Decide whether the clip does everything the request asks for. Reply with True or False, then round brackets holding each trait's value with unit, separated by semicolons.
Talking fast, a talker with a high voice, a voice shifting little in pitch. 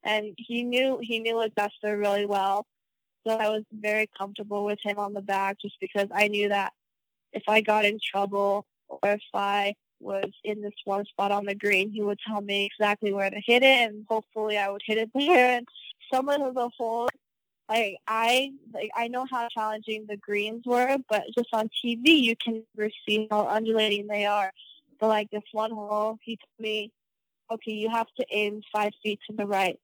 True (210 wpm; 215 Hz; 1.9 semitones)